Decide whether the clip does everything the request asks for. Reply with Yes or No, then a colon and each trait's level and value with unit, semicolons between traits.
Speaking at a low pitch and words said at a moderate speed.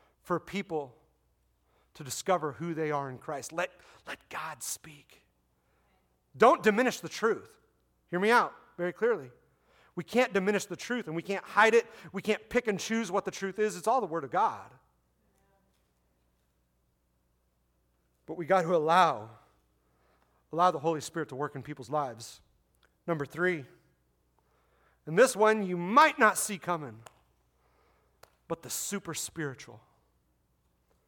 No: medium, 150 Hz; average, 145 wpm